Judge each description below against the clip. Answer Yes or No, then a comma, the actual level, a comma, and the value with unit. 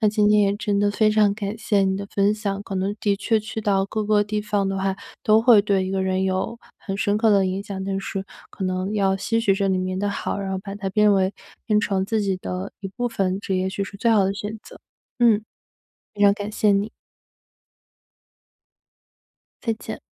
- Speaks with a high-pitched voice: Yes, high, 200 Hz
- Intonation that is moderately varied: No, narrow, 1.6 semitones